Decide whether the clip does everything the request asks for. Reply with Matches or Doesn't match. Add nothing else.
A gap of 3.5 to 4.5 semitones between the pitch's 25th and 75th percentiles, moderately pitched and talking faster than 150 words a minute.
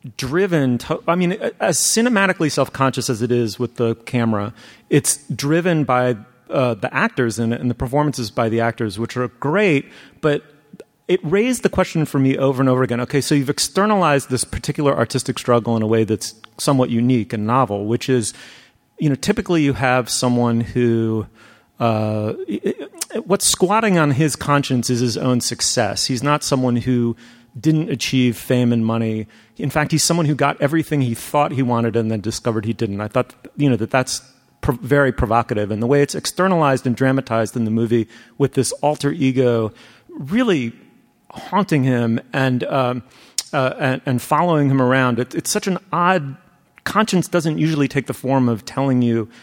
Doesn't match